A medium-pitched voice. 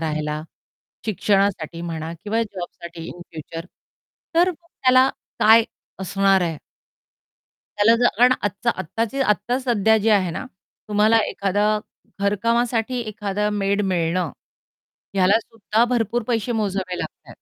No: high, 205 Hz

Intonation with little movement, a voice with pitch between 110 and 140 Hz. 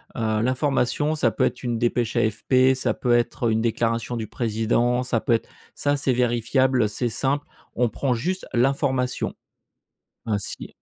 Yes: narrow, 2.3 semitones; low, 120 Hz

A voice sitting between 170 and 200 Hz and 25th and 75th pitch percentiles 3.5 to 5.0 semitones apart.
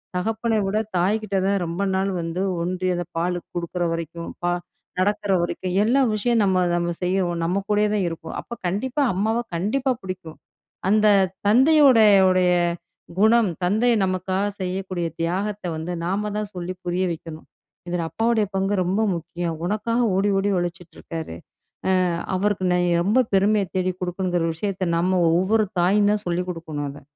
No: medium, 185 Hz; average, 3.1 semitones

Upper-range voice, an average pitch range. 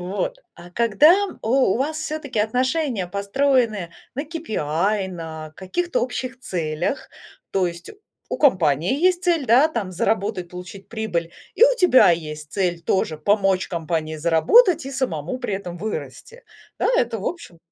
No: high, 205 Hz; wide, 7.8 semitones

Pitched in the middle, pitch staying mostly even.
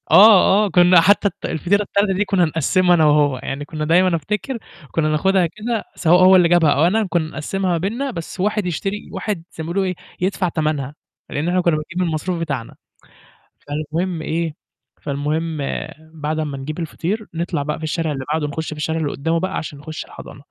No: medium, 165 Hz; average, 3.4 semitones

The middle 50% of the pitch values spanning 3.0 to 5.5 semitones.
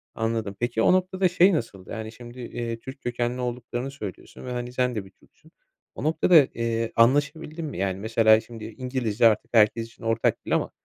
No: narrow, 2.5 semitones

